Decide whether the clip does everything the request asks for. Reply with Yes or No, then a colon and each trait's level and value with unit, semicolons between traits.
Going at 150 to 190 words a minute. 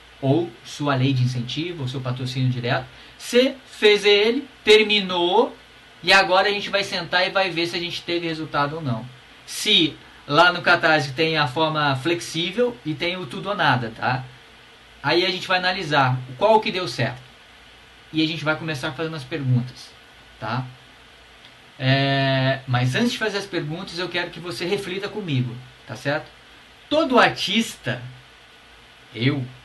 Yes: average, 160 wpm